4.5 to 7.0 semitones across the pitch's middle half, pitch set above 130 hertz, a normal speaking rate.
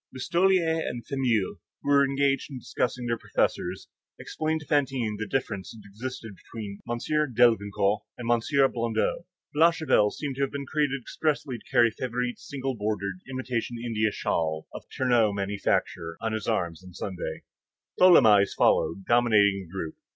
No: average, 4.9 semitones; low, 120 Hz; average, 150 wpm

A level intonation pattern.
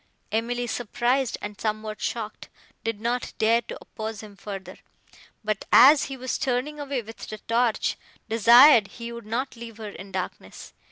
Yes: narrow, 2.3 semitones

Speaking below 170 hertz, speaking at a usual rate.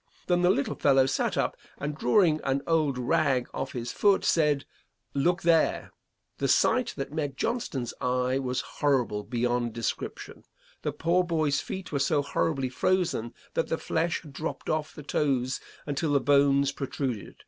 Yes: medium, 140 Hz; average, 160 wpm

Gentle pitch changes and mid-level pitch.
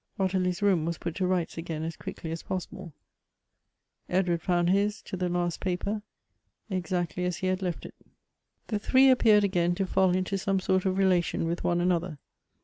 Yes: narrow, 1.6 semitones; medium, 180 Hz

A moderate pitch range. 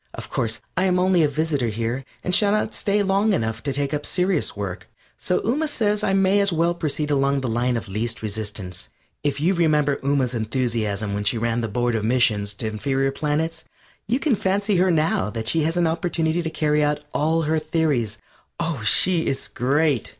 No: wide, 7.0 semitones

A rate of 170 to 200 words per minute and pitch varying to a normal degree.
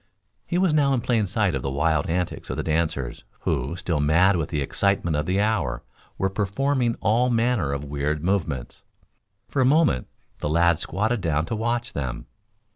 No: average, 185 wpm; wide, 7.6 semitones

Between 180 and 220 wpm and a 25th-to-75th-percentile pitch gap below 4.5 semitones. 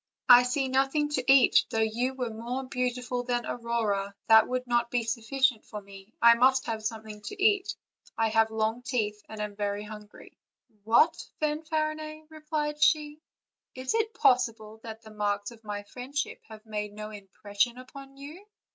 No: average, 165 wpm; average, 3.9 semitones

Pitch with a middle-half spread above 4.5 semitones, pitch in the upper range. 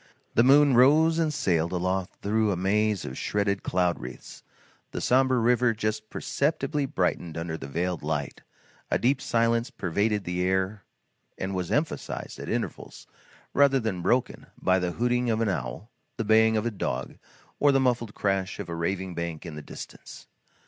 No: average, 5.3 semitones; low, 105 Hz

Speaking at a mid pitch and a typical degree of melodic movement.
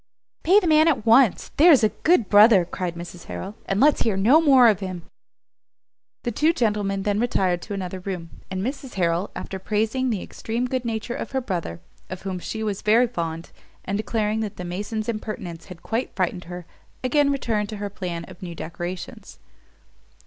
No: high, 210 Hz; average, 4.8 semitones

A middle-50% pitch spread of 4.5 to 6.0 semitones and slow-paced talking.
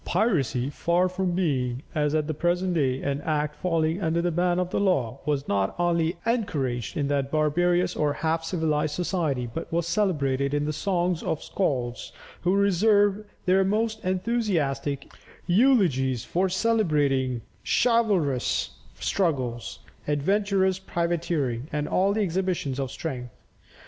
No: average, 5.0 semitones; average, 145 wpm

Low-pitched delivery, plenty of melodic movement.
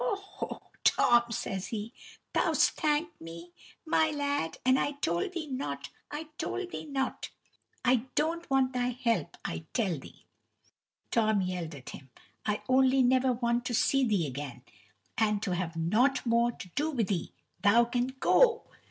No: high, 240 Hz; wide, 6.8 semitones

